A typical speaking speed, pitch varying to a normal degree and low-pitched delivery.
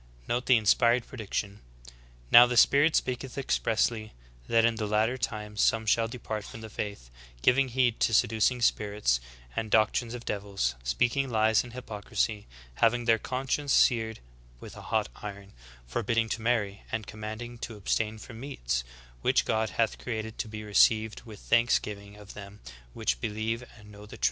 No: average, 165 wpm; narrow, 2.2 semitones; low, 110 Hz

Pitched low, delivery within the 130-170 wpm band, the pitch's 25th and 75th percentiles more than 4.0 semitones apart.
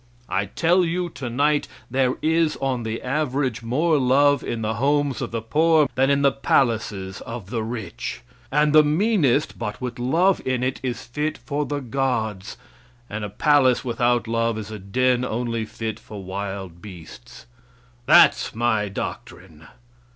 Yes: low, 125 Hz; average, 160 wpm; average, 4.7 semitones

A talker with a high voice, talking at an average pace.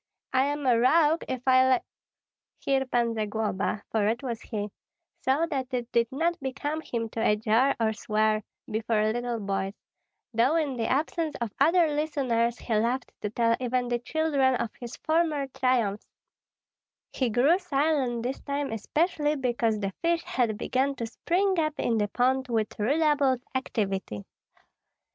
Yes: very high, 250 Hz; average, 160 wpm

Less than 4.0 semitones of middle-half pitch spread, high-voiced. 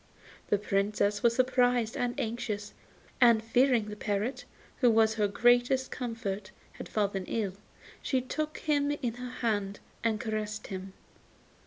Yes: average, 3.1 semitones; high, 225 Hz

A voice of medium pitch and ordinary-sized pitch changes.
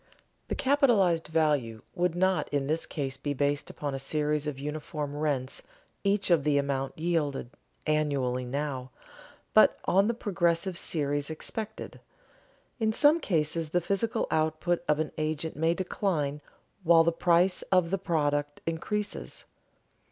Yes: medium, 155 Hz; average, 3.4 semitones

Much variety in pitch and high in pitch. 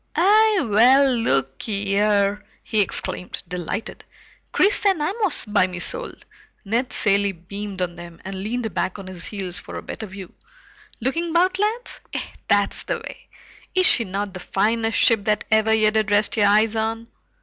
No: average, 3.9 semitones; high, 210 Hz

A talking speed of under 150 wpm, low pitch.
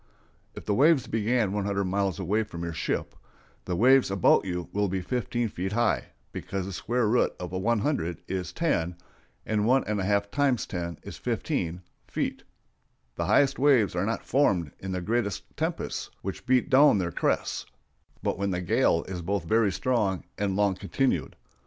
No: average, 175 wpm; low, 100 Hz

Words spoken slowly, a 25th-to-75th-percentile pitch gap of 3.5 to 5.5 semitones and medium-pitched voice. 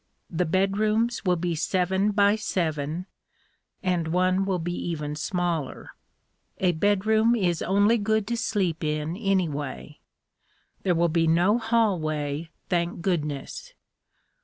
Yes: slow, 120 wpm; average, 4.0 semitones; medium, 180 Hz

